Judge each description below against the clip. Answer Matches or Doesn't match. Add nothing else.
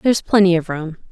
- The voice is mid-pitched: Matches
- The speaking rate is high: Matches